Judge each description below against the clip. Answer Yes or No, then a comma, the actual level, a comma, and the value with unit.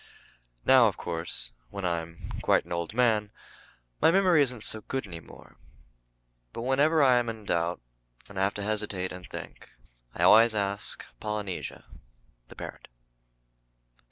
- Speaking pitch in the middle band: No, low, 105 Hz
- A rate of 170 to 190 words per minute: No, average, 150 wpm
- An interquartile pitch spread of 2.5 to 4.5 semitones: No, average, 5.1 semitones